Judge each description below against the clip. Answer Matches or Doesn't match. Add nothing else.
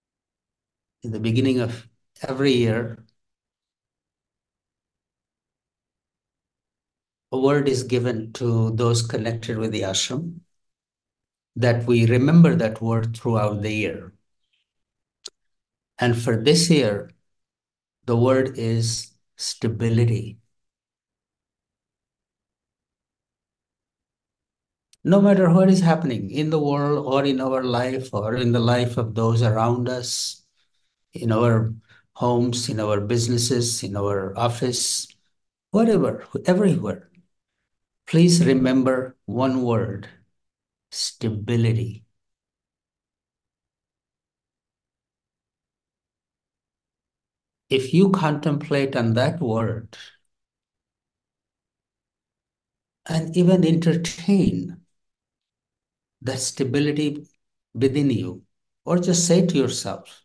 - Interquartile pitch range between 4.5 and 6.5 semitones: Doesn't match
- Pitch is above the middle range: Doesn't match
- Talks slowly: Matches